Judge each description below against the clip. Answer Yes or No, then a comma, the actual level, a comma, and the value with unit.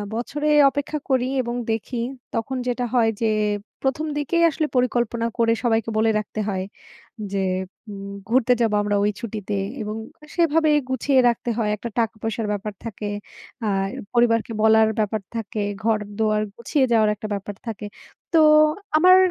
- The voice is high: Yes, high, 225 Hz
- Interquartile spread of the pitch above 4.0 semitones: No, average, 3.1 semitones